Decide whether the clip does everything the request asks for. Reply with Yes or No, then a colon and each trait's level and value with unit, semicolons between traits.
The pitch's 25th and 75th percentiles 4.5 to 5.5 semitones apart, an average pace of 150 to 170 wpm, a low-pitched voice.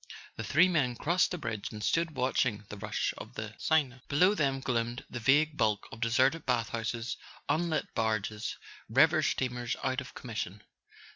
Yes: average, 5.2 semitones; average, 165 wpm; low, 125 Hz